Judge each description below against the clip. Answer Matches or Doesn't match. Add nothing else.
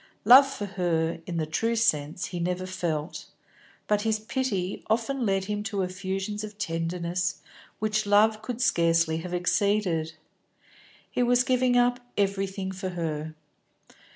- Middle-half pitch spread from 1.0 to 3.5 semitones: Doesn't match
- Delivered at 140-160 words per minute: Matches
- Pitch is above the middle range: Matches